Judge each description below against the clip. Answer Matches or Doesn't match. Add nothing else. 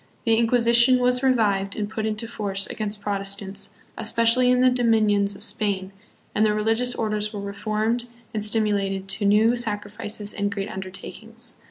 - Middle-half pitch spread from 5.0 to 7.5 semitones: Doesn't match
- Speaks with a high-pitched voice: Matches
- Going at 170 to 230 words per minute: Doesn't match